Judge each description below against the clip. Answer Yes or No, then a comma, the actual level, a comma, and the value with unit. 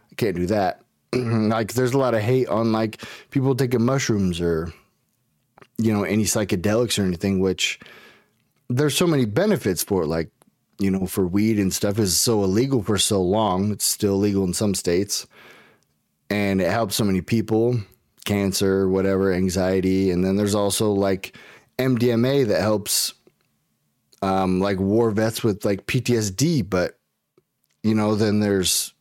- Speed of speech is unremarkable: Yes, average, 155 wpm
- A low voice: Yes, low, 105 Hz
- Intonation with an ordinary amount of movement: Yes, average, 3.3 semitones